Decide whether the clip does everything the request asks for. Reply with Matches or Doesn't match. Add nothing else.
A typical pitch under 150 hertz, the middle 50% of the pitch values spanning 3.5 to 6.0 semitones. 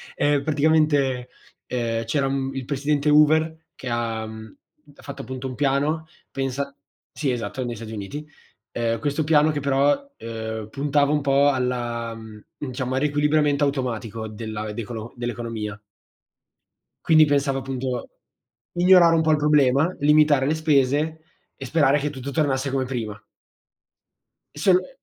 Matches